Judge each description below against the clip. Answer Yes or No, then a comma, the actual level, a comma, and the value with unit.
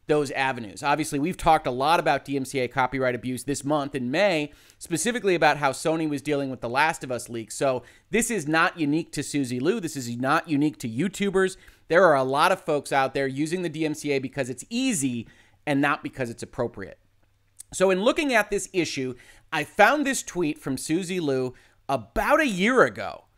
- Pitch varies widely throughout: No, average, 4.2 semitones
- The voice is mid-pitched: Yes, medium, 145 Hz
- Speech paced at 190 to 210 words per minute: Yes, average, 200 wpm